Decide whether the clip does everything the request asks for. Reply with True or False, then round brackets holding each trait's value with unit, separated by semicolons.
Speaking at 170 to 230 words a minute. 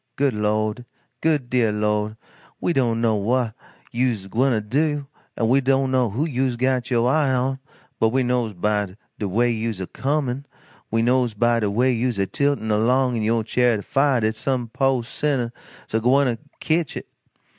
True (185 wpm)